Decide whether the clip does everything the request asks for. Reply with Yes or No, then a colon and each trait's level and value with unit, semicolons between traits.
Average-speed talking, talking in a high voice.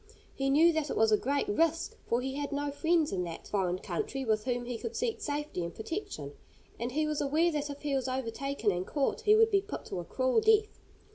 No: fast, 235 wpm; very high, 280 Hz